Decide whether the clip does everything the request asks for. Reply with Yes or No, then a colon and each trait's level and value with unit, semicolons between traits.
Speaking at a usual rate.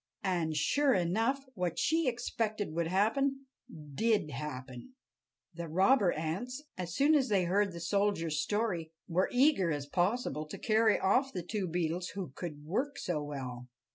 Yes: average, 160 wpm